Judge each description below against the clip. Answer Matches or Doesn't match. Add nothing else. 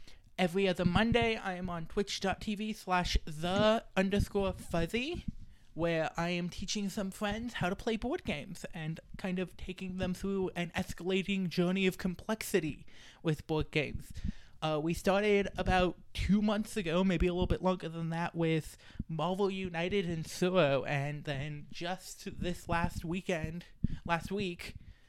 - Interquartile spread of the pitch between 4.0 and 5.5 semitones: Doesn't match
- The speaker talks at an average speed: Matches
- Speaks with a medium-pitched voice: Matches